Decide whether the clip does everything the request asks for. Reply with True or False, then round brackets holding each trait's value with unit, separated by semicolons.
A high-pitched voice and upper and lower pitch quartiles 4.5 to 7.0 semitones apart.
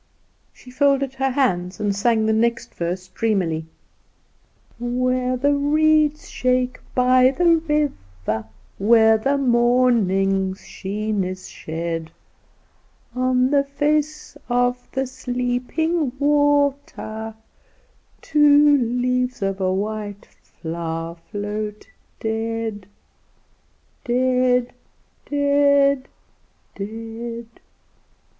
True (245 Hz; 5.0 semitones)